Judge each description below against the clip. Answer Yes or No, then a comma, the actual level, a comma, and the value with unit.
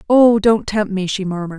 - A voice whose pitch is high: Yes, high, 200 Hz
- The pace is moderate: No, fast, 225 wpm